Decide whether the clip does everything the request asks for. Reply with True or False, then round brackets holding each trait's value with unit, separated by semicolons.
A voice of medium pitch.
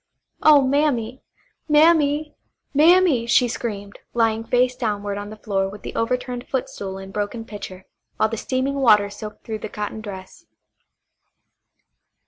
False (230 Hz)